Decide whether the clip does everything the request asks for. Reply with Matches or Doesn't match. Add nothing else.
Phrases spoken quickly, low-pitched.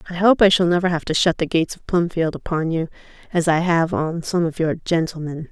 Doesn't match